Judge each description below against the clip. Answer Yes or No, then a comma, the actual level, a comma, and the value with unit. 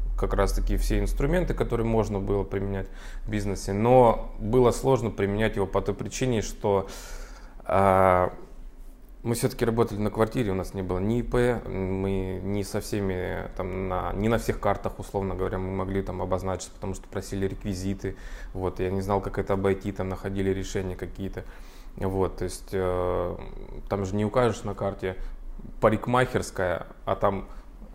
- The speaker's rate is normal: No, fast, 165 wpm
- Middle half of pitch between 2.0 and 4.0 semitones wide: Yes, narrow, 2.4 semitones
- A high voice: No, low, 100 Hz